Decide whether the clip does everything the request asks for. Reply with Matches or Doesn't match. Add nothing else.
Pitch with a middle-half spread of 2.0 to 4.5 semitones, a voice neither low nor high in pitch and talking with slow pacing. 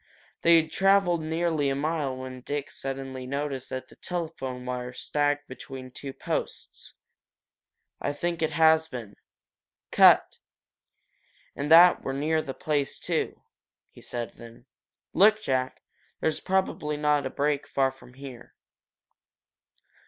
Matches